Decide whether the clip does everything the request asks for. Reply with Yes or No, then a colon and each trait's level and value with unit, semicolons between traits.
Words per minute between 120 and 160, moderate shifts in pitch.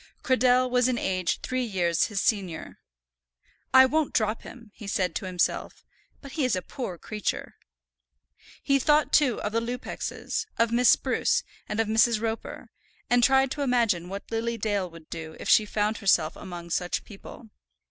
No: average, 170 wpm; average, 4.7 semitones